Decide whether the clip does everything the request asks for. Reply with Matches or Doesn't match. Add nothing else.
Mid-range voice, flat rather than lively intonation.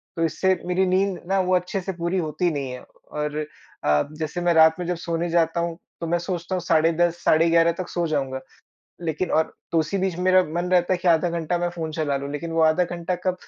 Matches